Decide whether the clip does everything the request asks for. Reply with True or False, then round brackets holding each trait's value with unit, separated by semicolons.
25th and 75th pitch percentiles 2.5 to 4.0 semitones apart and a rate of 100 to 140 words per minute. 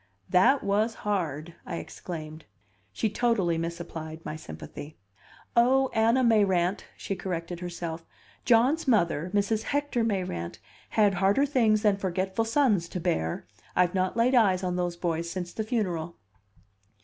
False (4.8 semitones; 135 wpm)